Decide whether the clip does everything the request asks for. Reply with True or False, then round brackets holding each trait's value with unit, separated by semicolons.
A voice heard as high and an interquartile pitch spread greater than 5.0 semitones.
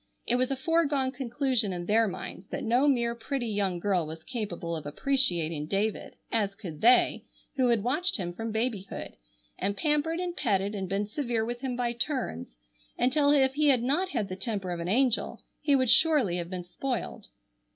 True (235 Hz; 5.6 semitones)